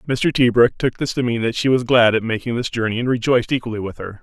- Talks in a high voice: No, low, 120 Hz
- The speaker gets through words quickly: Yes, fast, 270 wpm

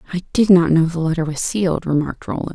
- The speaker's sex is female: Yes, female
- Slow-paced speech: No, fast, 235 wpm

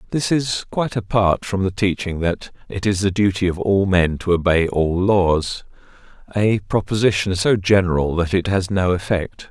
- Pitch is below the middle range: Yes, very low, 95 Hz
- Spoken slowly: No, average, 175 wpm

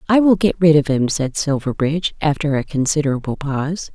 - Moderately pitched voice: Yes, medium, 150 Hz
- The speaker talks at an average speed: Yes, average, 180 wpm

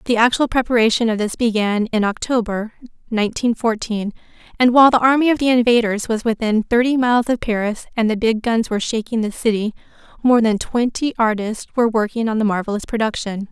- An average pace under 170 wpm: No, average, 180 wpm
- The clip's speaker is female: Yes, female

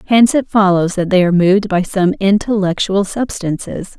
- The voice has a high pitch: Yes, high, 195 Hz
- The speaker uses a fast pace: No, average, 165 wpm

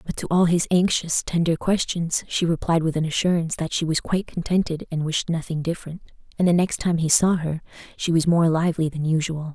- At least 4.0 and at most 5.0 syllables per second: No, 5.7 syllables/s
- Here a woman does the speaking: Yes, female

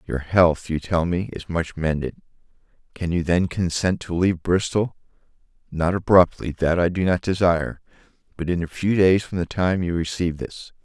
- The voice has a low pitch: Yes, very low, 90 Hz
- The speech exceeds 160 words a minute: Yes, average, 170 wpm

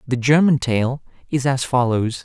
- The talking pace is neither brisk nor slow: Yes, average, 160 wpm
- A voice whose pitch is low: Yes, low, 130 Hz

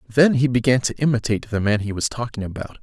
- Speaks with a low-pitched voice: Yes, low, 120 Hz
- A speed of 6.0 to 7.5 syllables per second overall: Yes, 6.5 syllables/s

